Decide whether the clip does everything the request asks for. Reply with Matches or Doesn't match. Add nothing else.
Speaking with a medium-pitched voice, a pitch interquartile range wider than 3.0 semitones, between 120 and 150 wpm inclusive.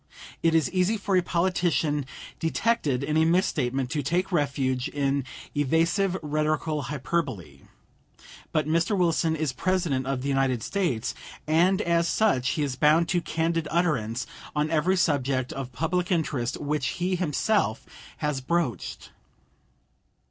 Matches